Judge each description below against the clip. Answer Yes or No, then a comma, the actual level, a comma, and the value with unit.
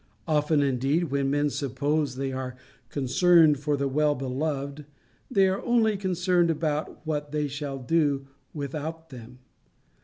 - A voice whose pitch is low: No, medium, 145 Hz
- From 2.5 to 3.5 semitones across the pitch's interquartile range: Yes, average, 2.9 semitones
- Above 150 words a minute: No, slow, 135 wpm